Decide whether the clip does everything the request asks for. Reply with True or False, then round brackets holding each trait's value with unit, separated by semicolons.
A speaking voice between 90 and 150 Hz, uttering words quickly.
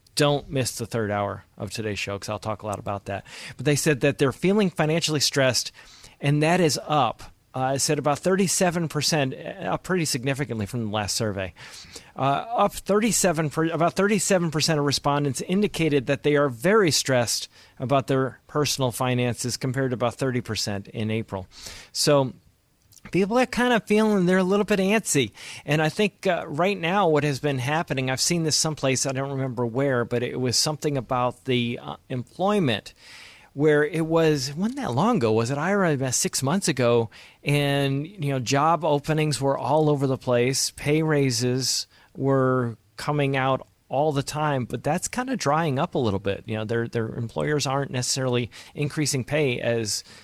False (140 Hz; 180 wpm)